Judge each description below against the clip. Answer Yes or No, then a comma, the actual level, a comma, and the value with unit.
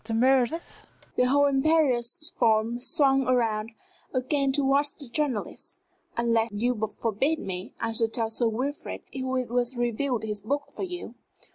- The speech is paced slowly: No, average, 150 wpm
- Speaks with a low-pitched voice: No, very high, 250 Hz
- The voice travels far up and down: No, average, 3.6 semitones